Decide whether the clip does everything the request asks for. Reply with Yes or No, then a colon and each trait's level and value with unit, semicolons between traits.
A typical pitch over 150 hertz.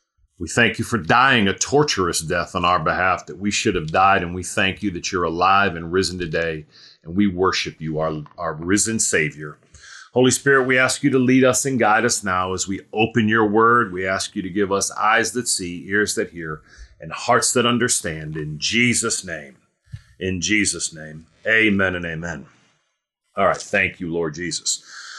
No: very low, 95 Hz